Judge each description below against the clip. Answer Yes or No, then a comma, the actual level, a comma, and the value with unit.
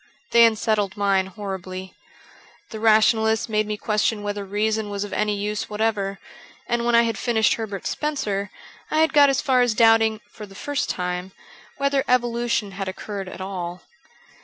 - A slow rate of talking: No, average, 165 wpm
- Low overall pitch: No, high, 215 Hz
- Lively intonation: No, average, 2.8 semitones